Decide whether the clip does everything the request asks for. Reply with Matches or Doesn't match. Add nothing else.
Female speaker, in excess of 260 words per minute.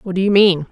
Matches